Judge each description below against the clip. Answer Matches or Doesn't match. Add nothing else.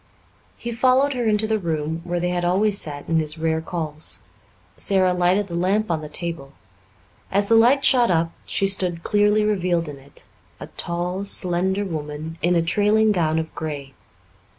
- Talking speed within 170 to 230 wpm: Matches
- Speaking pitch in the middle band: Matches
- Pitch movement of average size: Matches